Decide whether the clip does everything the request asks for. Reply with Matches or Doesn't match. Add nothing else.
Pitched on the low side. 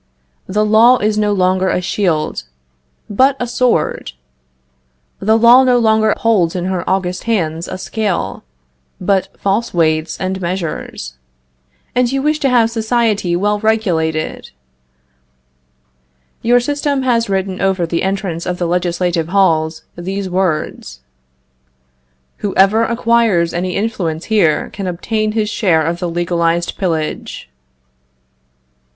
Doesn't match